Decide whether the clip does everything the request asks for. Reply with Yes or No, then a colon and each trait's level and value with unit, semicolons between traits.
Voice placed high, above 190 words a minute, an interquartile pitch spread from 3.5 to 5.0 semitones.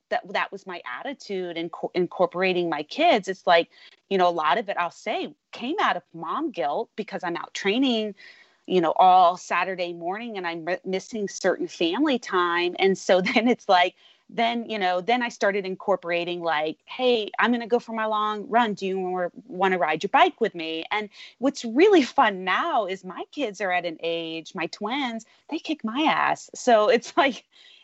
No: high, 200 Hz; average, 200 wpm; wide, 5.4 semitones